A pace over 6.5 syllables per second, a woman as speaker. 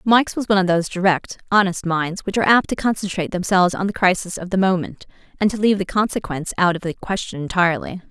Yes: 6.9 syllables/s; female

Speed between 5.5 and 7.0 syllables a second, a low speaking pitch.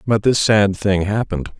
No: 4.9 syllables/s; low, 100 Hz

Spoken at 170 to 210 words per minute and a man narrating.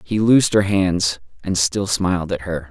Yes: average, 200 wpm; male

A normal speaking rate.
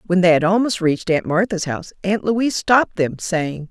No: fast, 210 wpm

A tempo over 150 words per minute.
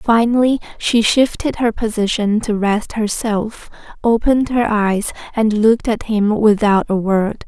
No: average, 145 wpm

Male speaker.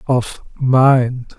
Yes: male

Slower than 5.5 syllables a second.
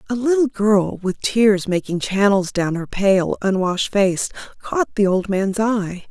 Yes: 4.0 syllables/s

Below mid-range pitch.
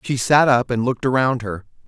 Yes: low, 125 Hz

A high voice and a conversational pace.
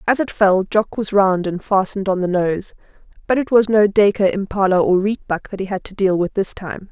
No: high, 195 Hz; fast, 235 wpm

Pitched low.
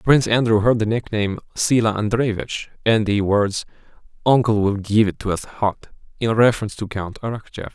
Yes: low, 110 Hz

